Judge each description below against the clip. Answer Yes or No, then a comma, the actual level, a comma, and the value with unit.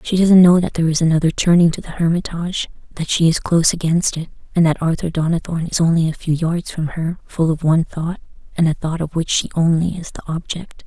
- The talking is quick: Yes, fast, 230 wpm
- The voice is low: No, medium, 165 Hz